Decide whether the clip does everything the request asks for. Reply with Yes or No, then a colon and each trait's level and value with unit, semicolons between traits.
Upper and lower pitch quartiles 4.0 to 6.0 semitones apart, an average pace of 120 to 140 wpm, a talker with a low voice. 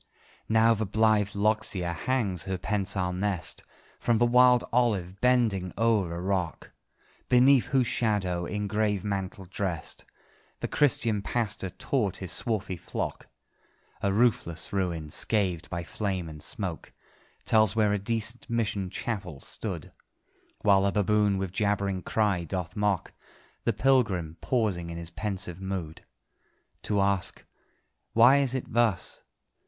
No: average, 3.3 semitones; slow, 135 wpm; low, 100 Hz